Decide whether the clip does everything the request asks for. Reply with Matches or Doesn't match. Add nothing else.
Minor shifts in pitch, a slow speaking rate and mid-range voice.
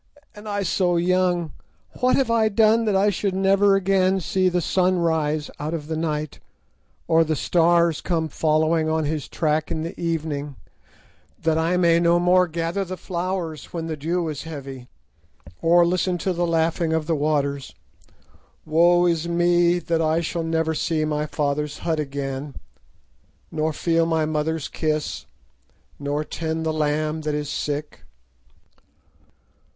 Doesn't match